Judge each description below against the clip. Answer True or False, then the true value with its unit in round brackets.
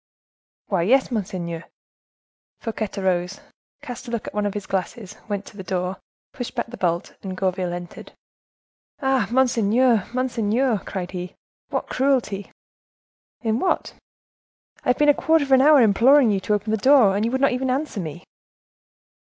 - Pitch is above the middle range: True (215 Hz)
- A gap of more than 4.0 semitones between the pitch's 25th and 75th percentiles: True (5.1 semitones)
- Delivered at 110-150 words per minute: False (165 wpm)